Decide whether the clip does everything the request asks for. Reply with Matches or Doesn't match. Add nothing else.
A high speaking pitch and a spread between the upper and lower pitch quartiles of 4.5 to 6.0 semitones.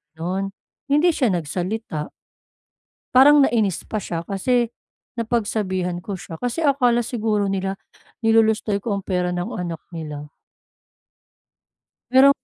Matches